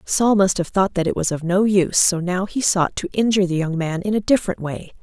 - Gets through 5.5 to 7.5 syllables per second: Yes, 5.8 syllables/s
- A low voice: No, medium, 185 Hz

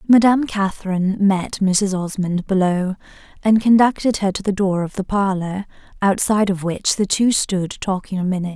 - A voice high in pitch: Yes, high, 195 Hz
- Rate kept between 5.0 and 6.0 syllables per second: Yes, 5.2 syllables/s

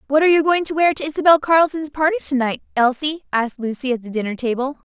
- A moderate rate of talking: No, fast, 230 wpm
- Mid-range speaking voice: No, very high, 285 Hz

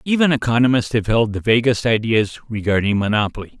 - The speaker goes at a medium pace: Yes, average, 150 wpm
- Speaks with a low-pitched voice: Yes, low, 115 Hz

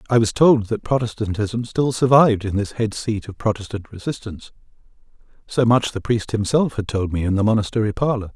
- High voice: No, low, 110 Hz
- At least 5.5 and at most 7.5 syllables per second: Yes, 5.7 syllables/s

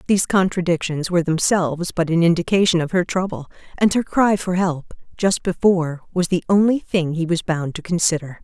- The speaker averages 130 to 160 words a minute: No, average, 185 wpm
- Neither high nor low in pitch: Yes, medium, 175 Hz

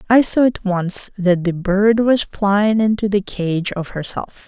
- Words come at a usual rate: Yes, average, 190 wpm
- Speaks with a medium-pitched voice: No, high, 200 Hz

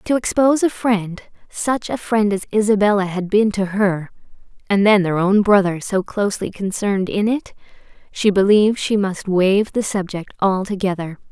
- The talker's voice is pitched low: No, high, 200 Hz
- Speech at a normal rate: Yes, average, 160 wpm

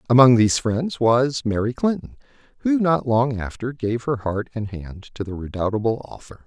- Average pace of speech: Yes, average, 175 wpm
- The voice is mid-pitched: No, low, 120 Hz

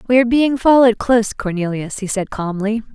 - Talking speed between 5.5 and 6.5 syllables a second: Yes, 6.0 syllables/s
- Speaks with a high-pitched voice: Yes, high, 225 Hz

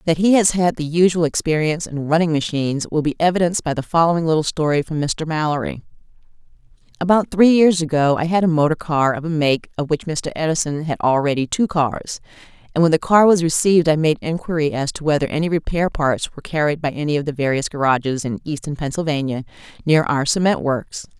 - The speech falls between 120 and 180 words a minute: No, average, 200 wpm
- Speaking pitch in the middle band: Yes, medium, 155 Hz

